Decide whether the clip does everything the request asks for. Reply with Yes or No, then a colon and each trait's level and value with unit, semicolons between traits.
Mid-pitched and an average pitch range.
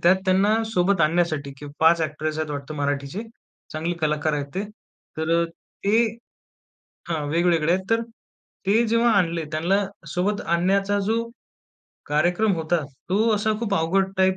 Yes: medium, 175 Hz; average, 4.2 semitones